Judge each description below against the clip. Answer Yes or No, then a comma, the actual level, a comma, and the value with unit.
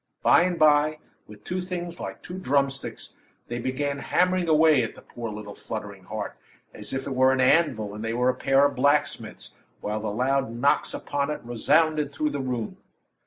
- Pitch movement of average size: Yes, average, 4.6 semitones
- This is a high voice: No, low, 135 Hz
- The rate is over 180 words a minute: Yes, average, 190 wpm